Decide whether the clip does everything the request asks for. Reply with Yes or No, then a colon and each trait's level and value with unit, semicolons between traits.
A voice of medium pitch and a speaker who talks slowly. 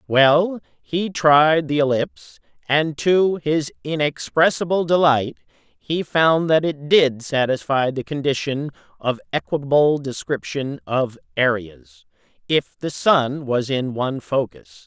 Yes: medium, 145 Hz; slow, 120 wpm